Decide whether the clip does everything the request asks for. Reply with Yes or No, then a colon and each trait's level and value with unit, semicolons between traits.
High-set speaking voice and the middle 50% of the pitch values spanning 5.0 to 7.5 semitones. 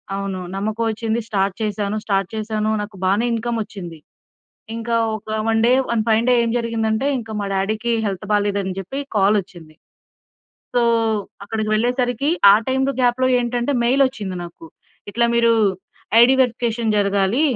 No: high, 220 Hz; average, 2.9 semitones